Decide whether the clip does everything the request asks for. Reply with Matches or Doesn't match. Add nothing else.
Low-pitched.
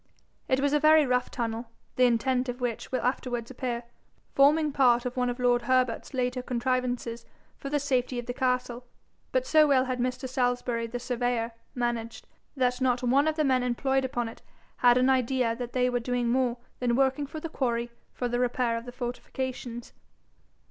Doesn't match